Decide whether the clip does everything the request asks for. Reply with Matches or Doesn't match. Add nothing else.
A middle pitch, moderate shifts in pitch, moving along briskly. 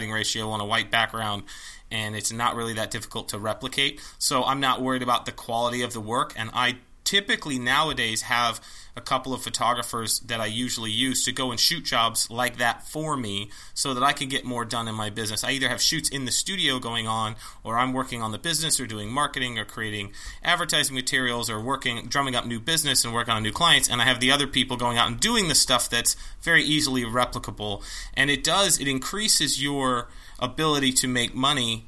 Doesn't match